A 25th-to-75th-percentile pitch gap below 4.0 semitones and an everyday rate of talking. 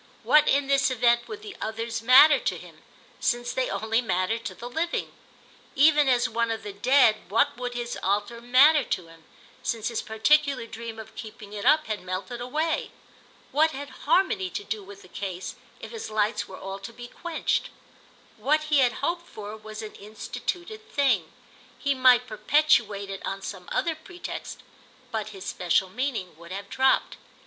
No: average, 5.3 semitones; average, 175 wpm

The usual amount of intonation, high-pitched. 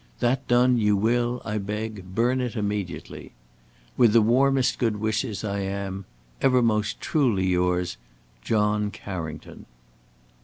No: average, 3.5 semitones; low, 105 Hz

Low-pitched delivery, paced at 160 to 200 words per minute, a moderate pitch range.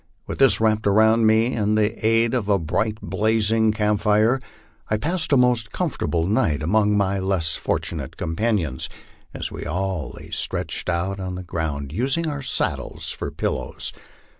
Yes: low, 105 Hz; average, 165 wpm; average, 3.2 semitones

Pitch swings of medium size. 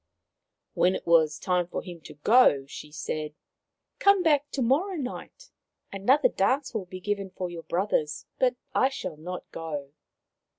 No: wide, 8.0 semitones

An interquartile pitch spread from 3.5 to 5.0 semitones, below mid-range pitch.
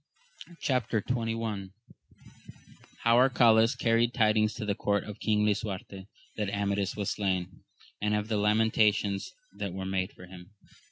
No: narrow, 2.4 semitones; low, 105 Hz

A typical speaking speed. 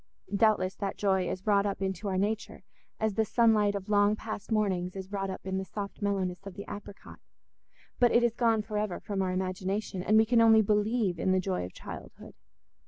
No: fast, 210 wpm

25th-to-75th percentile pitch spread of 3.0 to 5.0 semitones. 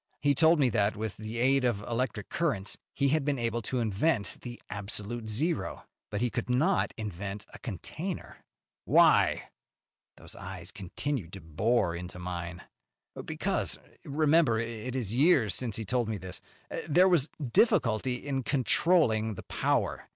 No: wide, 5.5 semitones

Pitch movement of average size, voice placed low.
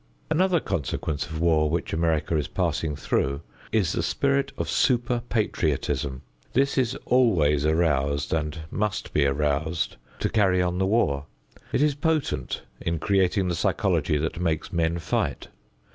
No: wide, 6.4 semitones; very low, 85 Hz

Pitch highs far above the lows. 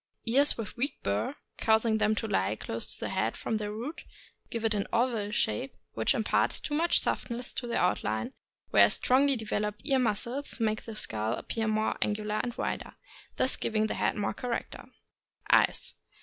No: narrow, 2.6 semitones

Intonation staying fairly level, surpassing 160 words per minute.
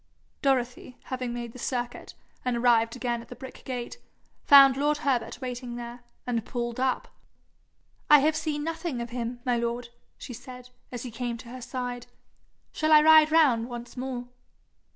Yes: narrow, 2.0 semitones; average, 170 wpm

